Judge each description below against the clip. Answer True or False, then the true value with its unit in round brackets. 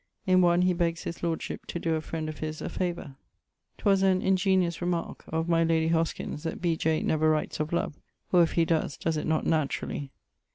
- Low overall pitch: False (165 Hz)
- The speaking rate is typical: False (210 wpm)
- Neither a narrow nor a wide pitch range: False (1.9 semitones)